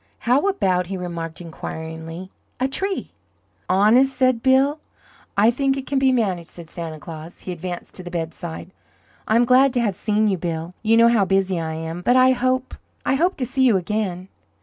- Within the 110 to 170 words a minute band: No, average, 190 wpm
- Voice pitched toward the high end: Yes, high, 200 Hz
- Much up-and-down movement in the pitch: Yes, wide, 6.8 semitones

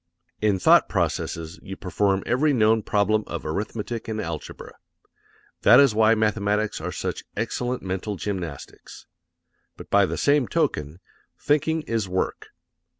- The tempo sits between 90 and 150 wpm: Yes, slow, 135 wpm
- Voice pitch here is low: Yes, low, 105 Hz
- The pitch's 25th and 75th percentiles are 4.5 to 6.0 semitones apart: No, average, 3.2 semitones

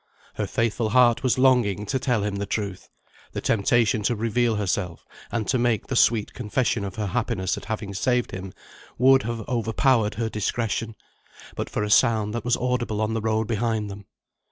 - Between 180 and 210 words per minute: Yes, average, 185 wpm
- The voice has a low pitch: Yes, low, 110 Hz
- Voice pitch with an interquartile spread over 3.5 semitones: No, narrow, 2.6 semitones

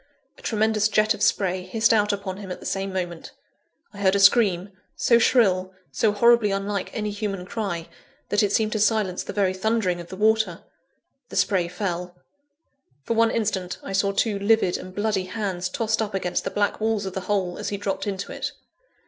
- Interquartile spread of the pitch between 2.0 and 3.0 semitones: Yes, narrow, 2.5 semitones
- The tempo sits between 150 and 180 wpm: No, average, 200 wpm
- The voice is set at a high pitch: Yes, high, 200 Hz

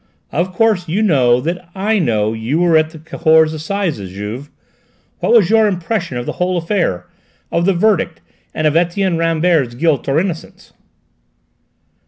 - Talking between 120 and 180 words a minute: Yes, average, 160 wpm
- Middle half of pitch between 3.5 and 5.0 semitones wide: Yes, average, 4.2 semitones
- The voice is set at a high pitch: No, medium, 165 Hz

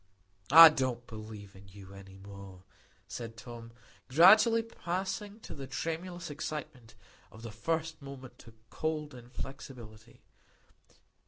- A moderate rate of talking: No, slow, 115 wpm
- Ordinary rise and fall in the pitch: No, wide, 6.5 semitones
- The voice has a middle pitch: No, low, 130 Hz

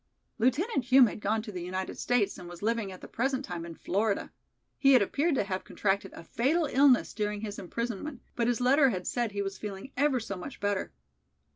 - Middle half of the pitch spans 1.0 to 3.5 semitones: No, average, 4.8 semitones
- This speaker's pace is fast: Yes, fast, 215 wpm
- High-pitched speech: Yes, high, 220 Hz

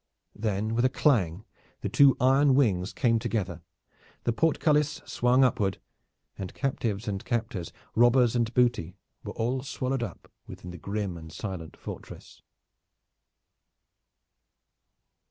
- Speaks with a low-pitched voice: Yes, low, 115 Hz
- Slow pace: Yes, slow, 120 wpm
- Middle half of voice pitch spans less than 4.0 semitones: No, average, 4.8 semitones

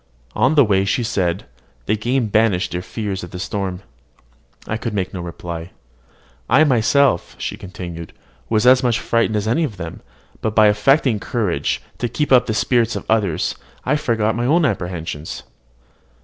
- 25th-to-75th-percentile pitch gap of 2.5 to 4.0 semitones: No, average, 4.7 semitones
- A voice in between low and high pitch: No, low, 110 Hz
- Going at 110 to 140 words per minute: No, average, 170 wpm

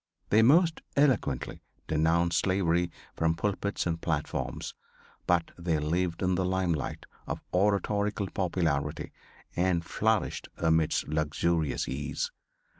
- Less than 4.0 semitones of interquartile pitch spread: Yes, average, 3.2 semitones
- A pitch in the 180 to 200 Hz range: No, very low, 85 Hz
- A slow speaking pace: Yes, slow, 110 wpm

